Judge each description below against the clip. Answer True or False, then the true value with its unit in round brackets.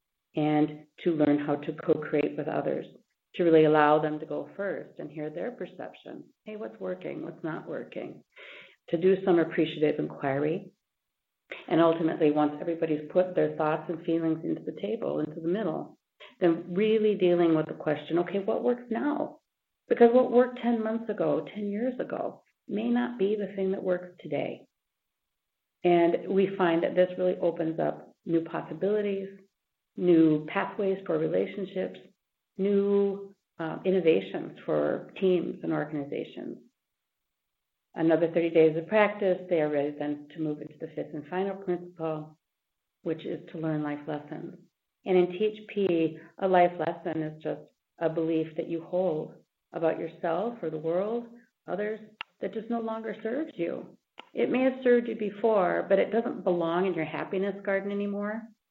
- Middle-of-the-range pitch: True (175 Hz)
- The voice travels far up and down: False (4.1 semitones)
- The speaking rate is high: False (160 wpm)